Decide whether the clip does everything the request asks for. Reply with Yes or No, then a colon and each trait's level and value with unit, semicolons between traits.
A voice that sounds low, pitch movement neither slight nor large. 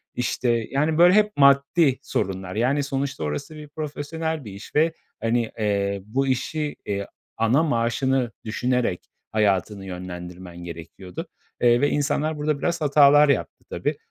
No: low, 130 Hz; wide, 6.7 semitones